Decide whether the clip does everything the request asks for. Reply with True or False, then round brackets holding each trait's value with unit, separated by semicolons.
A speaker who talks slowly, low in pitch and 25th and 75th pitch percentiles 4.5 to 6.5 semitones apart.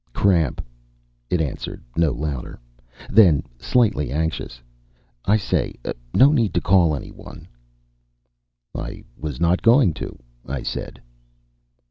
True (110 wpm; 85 Hz; 5.2 semitones)